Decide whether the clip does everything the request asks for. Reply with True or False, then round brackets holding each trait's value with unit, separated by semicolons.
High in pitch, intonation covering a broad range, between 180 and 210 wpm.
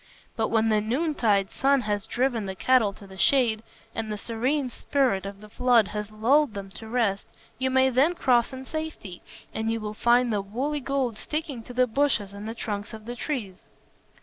False (230 Hz; 3.8 semitones; 200 wpm)